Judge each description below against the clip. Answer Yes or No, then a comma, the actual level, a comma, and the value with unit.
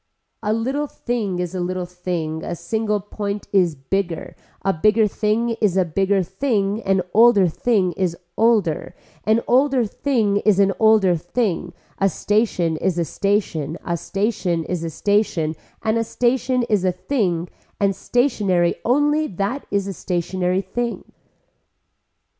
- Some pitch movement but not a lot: Yes, average, 3.9 semitones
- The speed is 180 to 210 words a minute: No, average, 145 wpm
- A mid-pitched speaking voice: No, high, 200 Hz